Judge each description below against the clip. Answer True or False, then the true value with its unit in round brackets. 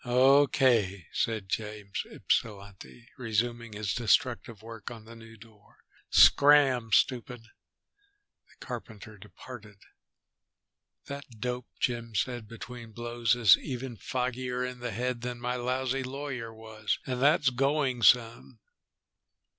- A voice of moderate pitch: False (120 Hz)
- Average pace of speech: False (115 wpm)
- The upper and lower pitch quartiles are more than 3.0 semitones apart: False (2.4 semitones)